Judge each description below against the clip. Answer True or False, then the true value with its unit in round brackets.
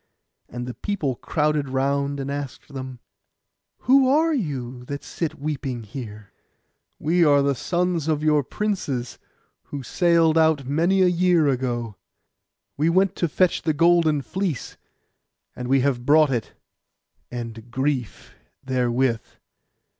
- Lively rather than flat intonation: False (4.7 semitones)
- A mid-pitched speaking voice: True (145 Hz)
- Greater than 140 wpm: False (135 wpm)